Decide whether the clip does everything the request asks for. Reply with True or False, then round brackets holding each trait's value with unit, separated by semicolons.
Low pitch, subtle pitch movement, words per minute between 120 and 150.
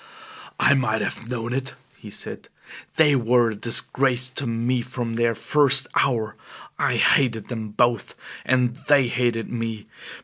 True (120 Hz; 2.3 semitones; 145 wpm)